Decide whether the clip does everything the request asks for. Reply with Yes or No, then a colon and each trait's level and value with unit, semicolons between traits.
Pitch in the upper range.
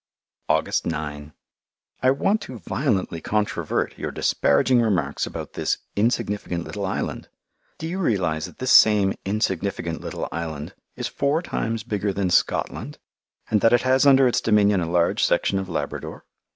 No: low, 105 Hz